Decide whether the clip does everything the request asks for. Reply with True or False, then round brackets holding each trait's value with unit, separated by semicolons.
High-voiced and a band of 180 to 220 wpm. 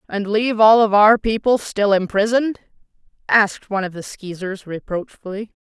False (210 Hz; 150 wpm)